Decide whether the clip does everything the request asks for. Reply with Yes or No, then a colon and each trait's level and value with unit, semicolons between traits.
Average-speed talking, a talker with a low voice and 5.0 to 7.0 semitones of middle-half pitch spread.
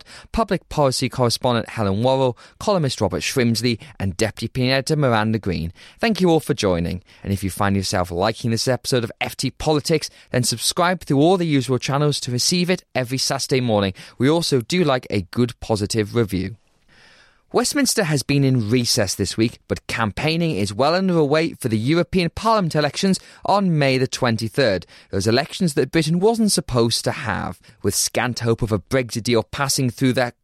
Yes: average, 175 wpm; low, 130 Hz; wide, 5.6 semitones